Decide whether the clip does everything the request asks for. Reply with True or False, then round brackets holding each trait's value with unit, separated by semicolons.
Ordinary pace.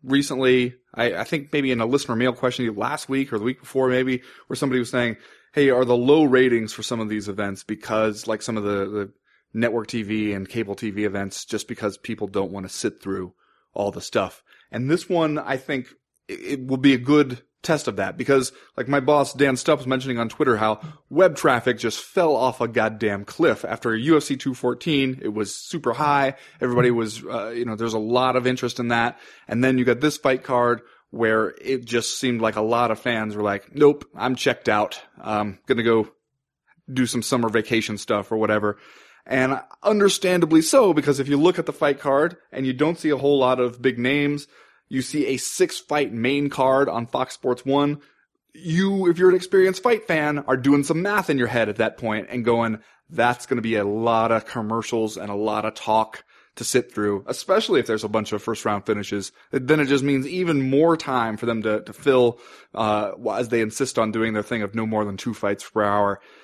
False (220 wpm)